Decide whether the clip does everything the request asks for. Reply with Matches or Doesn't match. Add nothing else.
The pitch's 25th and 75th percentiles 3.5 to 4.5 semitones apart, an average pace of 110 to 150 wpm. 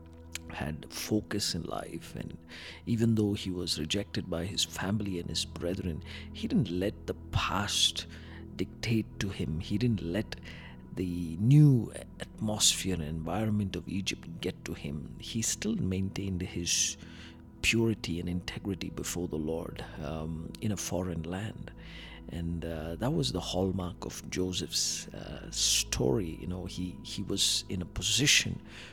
Matches